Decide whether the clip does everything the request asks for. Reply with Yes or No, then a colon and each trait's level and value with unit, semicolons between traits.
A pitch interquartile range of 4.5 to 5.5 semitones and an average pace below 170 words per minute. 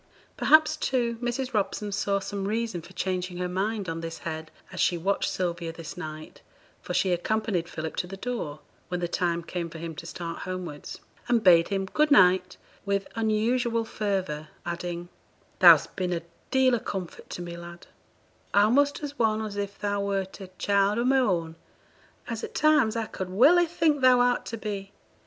No: average, 4.8 semitones; average, 185 wpm